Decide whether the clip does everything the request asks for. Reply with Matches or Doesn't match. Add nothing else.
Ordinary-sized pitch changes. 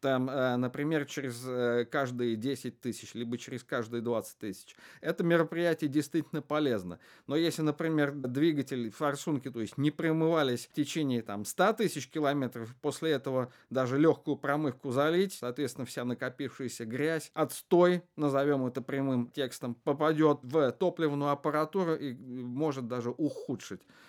Matches